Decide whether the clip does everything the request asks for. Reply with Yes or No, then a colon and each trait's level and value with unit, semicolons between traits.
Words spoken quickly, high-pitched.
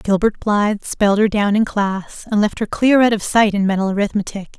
Yes: fast, 220 wpm; high, 205 Hz